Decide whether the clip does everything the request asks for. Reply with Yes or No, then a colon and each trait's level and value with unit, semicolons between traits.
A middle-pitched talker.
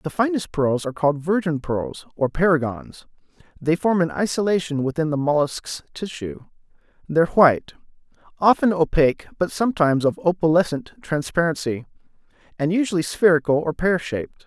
Yes: medium, 160 Hz